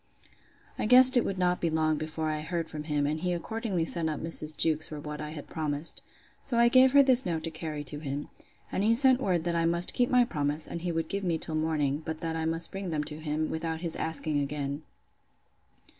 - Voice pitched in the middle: Yes, medium, 160 Hz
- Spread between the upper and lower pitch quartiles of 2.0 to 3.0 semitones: Yes, average, 2.7 semitones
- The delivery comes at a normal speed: No, fast, 235 wpm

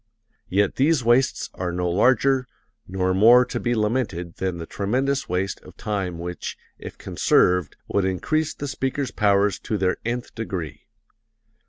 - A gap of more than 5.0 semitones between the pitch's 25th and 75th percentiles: Yes, wide, 5.5 semitones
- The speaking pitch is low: Yes, low, 105 Hz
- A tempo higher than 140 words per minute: Yes, average, 150 wpm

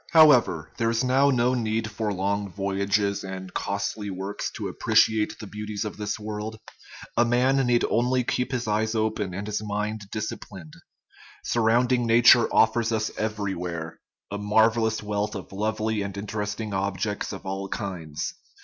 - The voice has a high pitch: No, low, 105 Hz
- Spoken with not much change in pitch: Yes, narrow, 2.3 semitones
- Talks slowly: No, average, 155 wpm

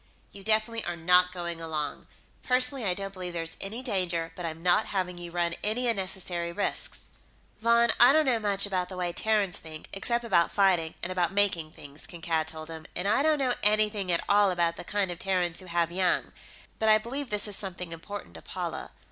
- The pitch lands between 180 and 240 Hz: Yes, medium, 185 Hz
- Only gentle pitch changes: No, average, 3.8 semitones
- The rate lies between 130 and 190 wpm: No, fast, 205 wpm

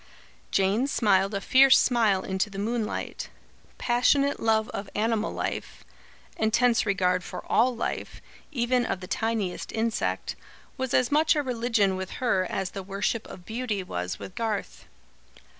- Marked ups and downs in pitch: No, average, 3.9 semitones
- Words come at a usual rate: Yes, average, 145 wpm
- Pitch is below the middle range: No, high, 220 Hz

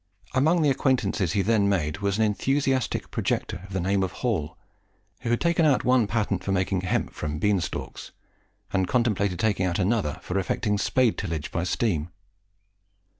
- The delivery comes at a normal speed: Yes, average, 175 wpm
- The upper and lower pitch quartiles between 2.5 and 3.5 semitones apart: No, average, 4.5 semitones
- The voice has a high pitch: No, low, 100 Hz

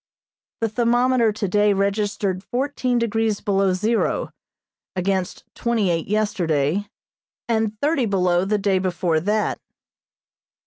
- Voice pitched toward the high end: Yes, high, 205 Hz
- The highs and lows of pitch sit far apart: No, average, 3.2 semitones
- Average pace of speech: No, slow, 105 wpm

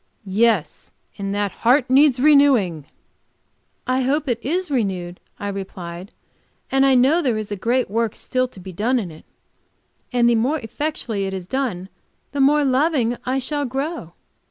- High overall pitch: Yes, high, 245 Hz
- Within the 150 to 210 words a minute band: Yes, average, 165 wpm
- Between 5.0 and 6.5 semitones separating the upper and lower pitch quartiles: Yes, wide, 5.5 semitones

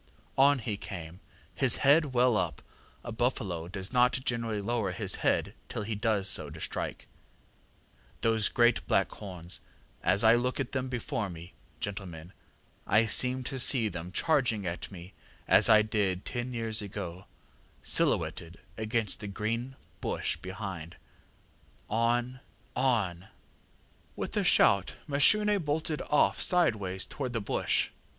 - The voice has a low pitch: Yes, low, 110 Hz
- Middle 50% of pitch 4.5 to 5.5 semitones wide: Yes, average, 4.8 semitones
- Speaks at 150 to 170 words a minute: No, average, 140 wpm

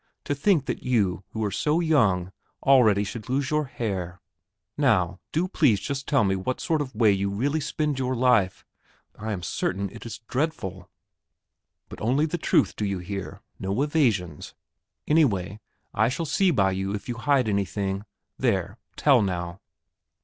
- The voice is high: No, low, 110 Hz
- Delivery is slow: No, average, 165 wpm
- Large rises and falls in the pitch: Yes, wide, 6.4 semitones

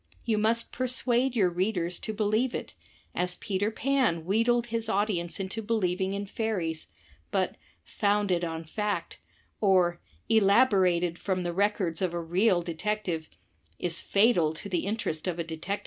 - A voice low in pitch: No, high, 195 Hz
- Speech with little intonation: No, average, 4.0 semitones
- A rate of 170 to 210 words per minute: No, average, 155 wpm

